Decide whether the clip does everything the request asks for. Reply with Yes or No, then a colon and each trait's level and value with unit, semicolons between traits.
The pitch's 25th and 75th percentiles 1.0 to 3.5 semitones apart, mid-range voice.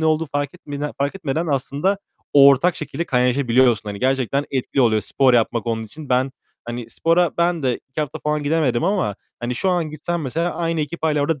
No: average, 4.4 semitones; medium, 145 Hz